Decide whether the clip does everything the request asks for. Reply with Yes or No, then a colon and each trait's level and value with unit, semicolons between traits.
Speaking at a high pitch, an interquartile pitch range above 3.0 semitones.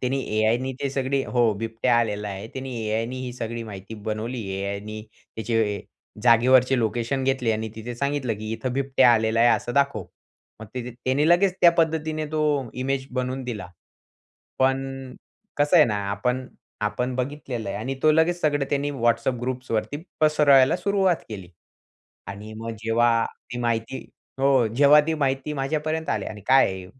No: low, 125 Hz; average, 3.5 semitones